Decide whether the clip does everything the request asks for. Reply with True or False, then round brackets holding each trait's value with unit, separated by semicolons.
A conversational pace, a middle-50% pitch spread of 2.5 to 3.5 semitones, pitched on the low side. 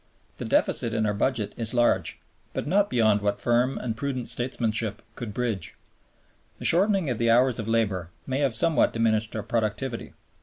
True (175 wpm; 2.8 semitones; 115 Hz)